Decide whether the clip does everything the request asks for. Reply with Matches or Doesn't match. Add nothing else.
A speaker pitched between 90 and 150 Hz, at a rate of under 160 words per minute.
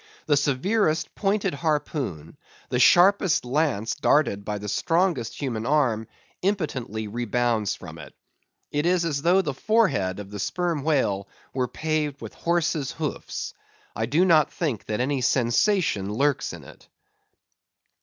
Matches